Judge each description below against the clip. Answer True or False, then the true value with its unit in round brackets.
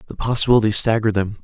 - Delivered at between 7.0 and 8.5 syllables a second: True (8.1 syllables/s)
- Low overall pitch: True (110 Hz)